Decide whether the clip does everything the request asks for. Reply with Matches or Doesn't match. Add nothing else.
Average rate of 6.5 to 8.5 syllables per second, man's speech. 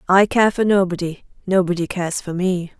Doesn't match